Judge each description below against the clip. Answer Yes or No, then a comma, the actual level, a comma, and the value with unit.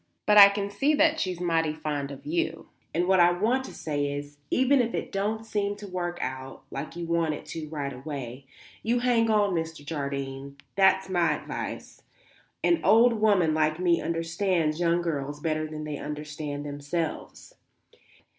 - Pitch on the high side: No, medium, 165 Hz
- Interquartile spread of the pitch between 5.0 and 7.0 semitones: Yes, wide, 5.4 semitones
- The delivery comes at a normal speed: Yes, average, 175 wpm